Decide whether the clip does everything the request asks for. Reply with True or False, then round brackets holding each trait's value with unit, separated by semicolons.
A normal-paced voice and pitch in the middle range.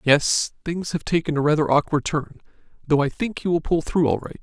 False (230 wpm; 155 Hz)